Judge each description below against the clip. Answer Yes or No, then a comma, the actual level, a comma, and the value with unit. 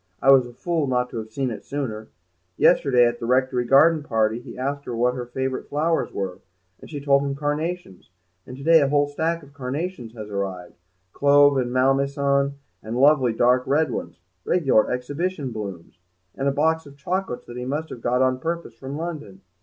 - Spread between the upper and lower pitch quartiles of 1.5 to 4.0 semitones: Yes, average, 3.2 semitones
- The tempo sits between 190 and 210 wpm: Yes, average, 195 wpm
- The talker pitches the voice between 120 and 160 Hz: Yes, low, 135 Hz